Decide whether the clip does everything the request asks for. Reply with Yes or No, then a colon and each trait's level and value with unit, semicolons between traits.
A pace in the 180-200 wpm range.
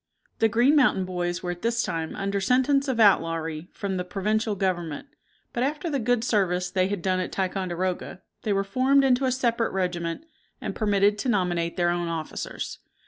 Yes: average, 185 wpm